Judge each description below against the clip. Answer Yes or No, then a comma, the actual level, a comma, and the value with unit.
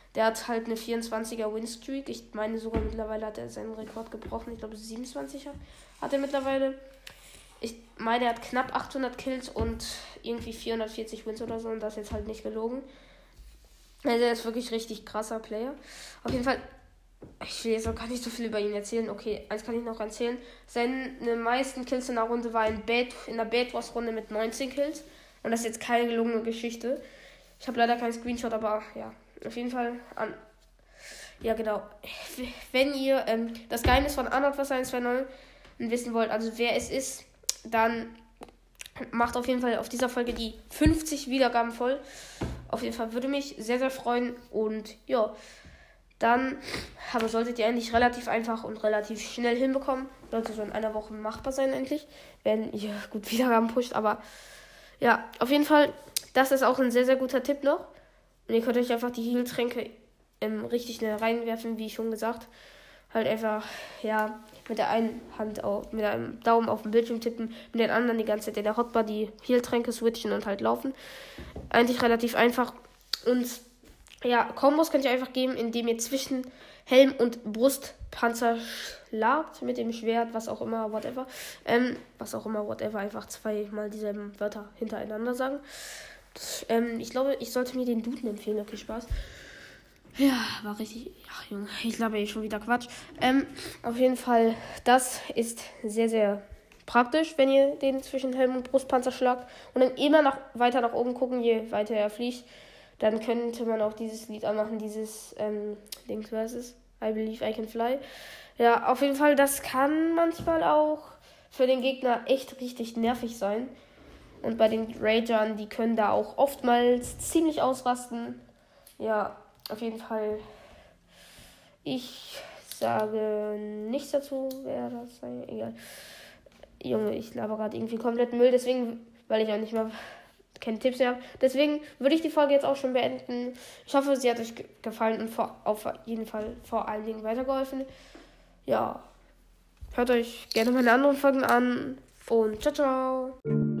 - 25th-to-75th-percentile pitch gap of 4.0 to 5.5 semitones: No, average, 2.7 semitones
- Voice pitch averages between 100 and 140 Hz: No, high, 235 Hz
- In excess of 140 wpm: Yes, average, 175 wpm